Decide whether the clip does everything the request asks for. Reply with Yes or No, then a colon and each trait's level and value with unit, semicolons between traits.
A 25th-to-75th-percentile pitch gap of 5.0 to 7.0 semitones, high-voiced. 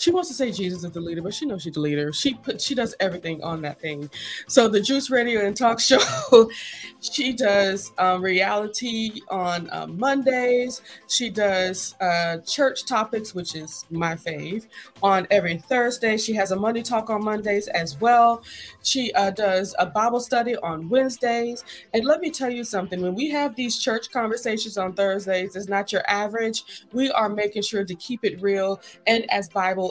No: average, 4.5 semitones; high, 210 Hz